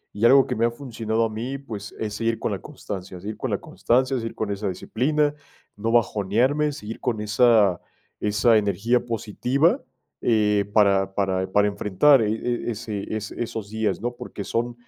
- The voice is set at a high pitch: No, low, 110 Hz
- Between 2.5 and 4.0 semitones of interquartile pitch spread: Yes, average, 2.8 semitones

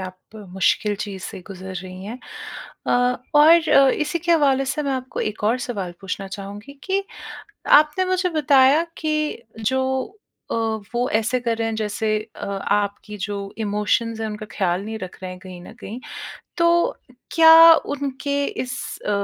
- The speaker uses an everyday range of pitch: No, wide, 5.9 semitones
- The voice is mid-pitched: No, high, 230 Hz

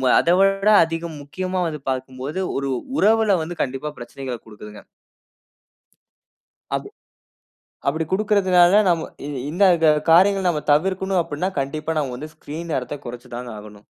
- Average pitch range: No, wide, 5.8 semitones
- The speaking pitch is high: No, medium, 160 Hz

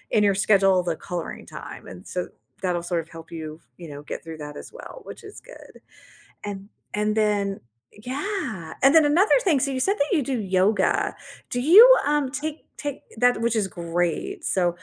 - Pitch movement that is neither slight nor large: No, wide, 8.8 semitones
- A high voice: Yes, high, 210 Hz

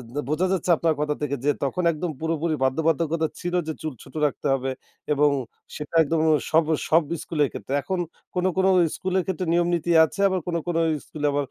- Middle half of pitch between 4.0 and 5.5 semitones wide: No, average, 2.7 semitones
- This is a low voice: No, medium, 160 Hz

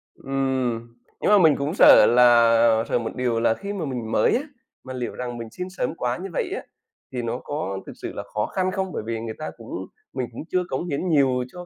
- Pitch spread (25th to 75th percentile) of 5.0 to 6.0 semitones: Yes, average, 5.3 semitones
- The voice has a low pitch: Yes, low, 125 Hz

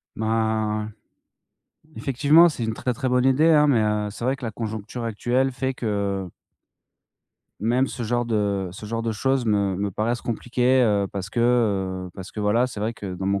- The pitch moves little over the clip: No, average, 3.4 semitones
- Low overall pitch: Yes, low, 110 Hz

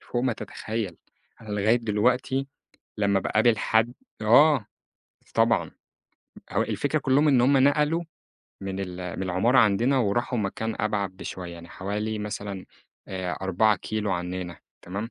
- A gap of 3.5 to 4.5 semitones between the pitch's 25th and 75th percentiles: Yes, average, 4.1 semitones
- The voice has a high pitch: No, low, 105 Hz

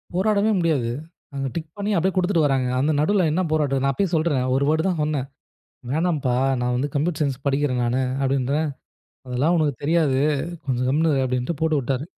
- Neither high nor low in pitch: Yes, medium, 145 Hz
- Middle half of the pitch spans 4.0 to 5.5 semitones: No, average, 3.6 semitones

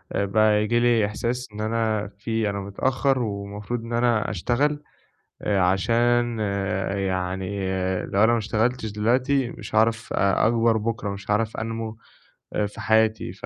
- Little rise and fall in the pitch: Yes, narrow, 2.3 semitones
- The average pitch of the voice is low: Yes, low, 110 Hz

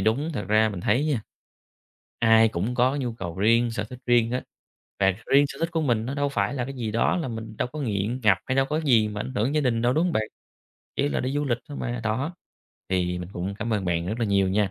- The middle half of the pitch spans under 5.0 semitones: Yes, average, 4.3 semitones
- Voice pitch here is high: No, low, 115 Hz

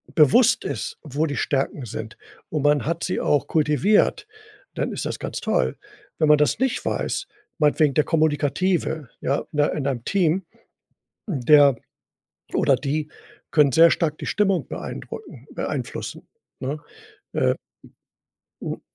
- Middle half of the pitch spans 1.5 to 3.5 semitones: Yes, average, 2.9 semitones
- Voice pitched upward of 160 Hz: No, medium, 150 Hz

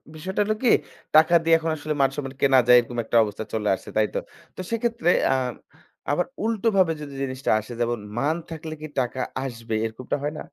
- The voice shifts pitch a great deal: Yes, wide, 5.9 semitones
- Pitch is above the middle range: No, medium, 145 Hz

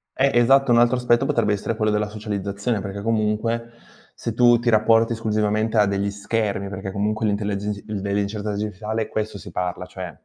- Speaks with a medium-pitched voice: No, low, 105 Hz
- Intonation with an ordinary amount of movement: No, narrow, 2.1 semitones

